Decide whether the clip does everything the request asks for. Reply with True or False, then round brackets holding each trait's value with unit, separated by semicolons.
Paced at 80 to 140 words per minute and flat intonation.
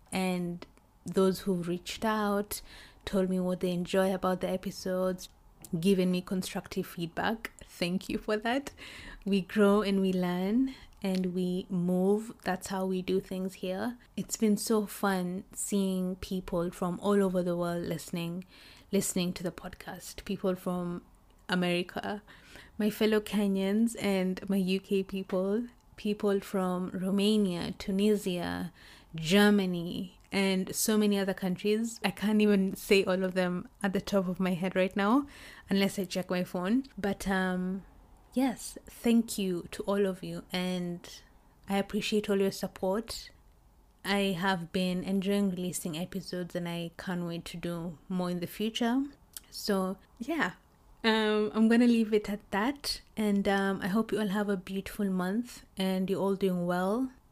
False (155 wpm; 2.0 semitones)